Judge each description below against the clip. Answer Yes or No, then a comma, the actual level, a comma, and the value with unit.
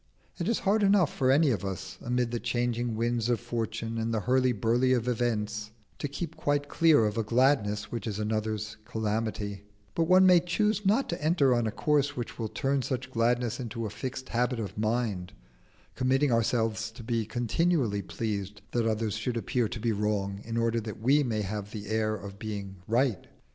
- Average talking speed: Yes, average, 195 wpm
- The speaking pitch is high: No, low, 115 Hz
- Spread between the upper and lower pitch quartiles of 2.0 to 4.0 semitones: Yes, average, 3.2 semitones